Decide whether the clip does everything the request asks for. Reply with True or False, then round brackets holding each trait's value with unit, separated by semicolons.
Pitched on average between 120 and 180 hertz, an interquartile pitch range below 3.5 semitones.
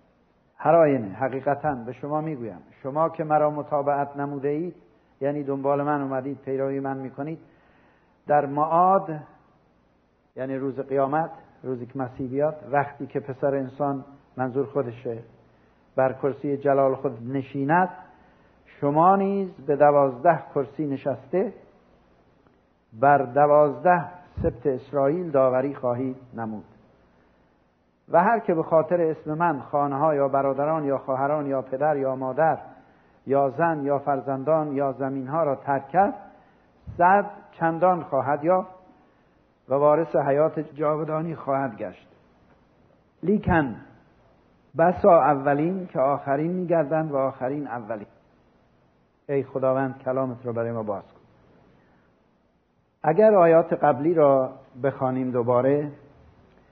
True (140 Hz; 3.1 semitones)